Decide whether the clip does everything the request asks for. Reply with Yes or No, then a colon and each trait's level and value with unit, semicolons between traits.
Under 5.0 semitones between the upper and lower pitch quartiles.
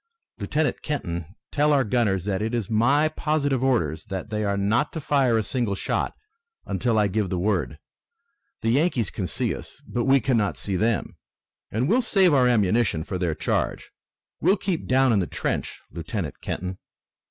No: wide, 5.6 semitones